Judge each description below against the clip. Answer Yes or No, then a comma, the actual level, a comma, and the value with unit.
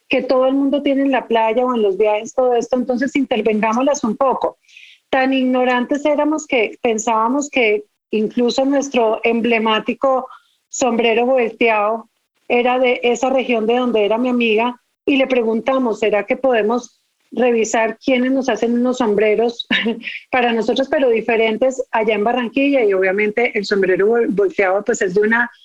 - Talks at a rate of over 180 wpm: No, average, 155 wpm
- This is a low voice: No, high, 240 Hz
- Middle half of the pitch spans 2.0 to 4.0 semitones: Yes, narrow, 2.6 semitones